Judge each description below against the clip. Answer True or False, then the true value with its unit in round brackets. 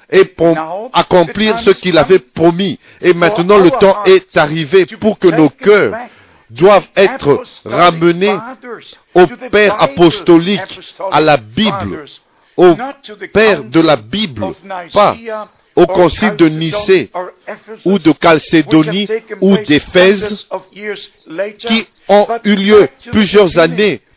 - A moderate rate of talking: False (115 wpm)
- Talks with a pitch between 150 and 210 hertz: True (190 Hz)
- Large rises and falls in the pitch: False (3.4 semitones)